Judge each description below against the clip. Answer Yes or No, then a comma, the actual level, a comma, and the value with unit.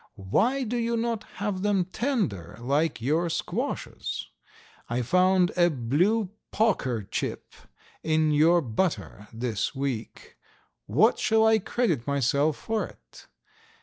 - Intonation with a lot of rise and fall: Yes, wide, 8.9 semitones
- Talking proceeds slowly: Yes, slow, 120 wpm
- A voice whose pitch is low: No, medium, 165 Hz